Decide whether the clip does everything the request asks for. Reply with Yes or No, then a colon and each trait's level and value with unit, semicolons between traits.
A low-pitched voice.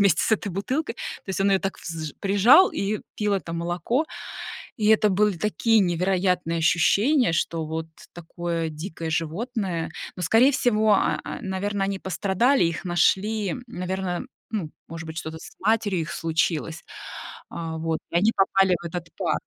No: high, 190 Hz